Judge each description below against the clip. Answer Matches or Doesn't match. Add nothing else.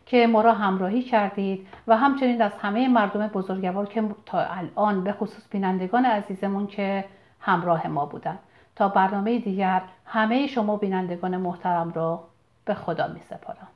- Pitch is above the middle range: Matches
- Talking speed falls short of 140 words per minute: Doesn't match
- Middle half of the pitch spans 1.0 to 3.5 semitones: Matches